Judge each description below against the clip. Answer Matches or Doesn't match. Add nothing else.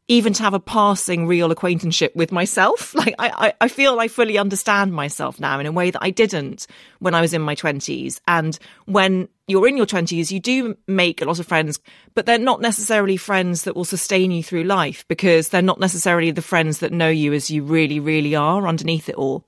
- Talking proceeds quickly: Matches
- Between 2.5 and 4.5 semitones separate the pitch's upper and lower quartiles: Matches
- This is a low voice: Doesn't match